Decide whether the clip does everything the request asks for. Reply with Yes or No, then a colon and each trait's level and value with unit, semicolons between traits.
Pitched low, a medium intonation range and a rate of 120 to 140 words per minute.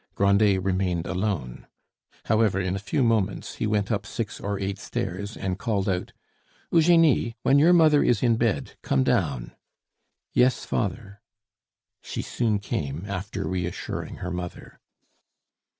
Yes: low, 100 Hz; average, 3.6 semitones; slow, 135 wpm